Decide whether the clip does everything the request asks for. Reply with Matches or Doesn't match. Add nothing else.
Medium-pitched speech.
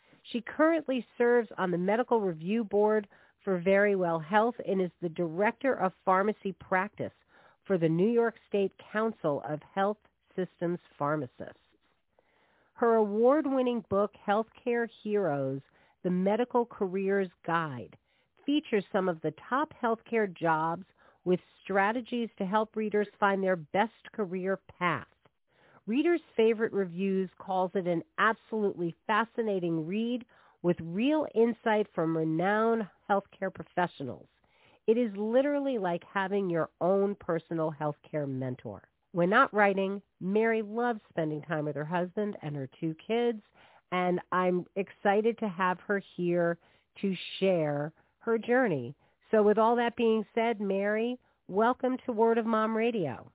Doesn't match